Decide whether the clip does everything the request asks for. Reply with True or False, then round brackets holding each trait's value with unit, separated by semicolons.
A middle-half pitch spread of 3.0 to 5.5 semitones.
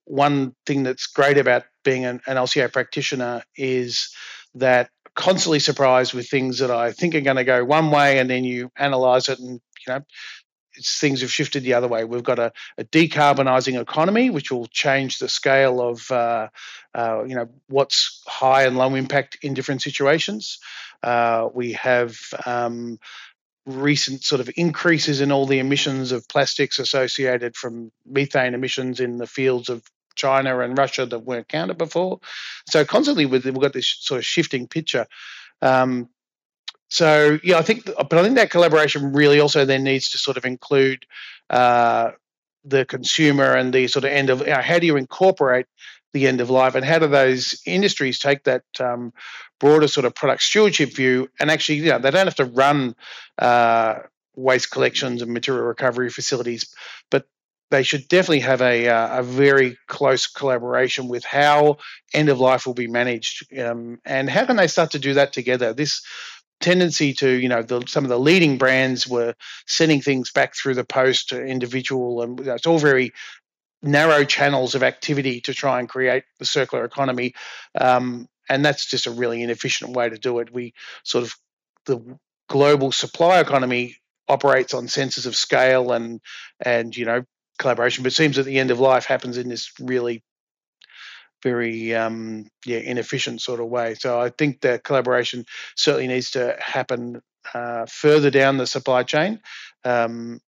False (2.5 semitones)